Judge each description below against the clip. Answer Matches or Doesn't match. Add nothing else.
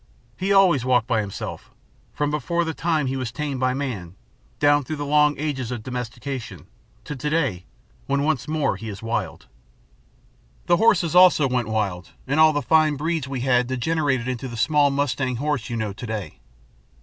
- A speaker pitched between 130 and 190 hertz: Matches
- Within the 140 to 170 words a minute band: Doesn't match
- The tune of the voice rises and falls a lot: Doesn't match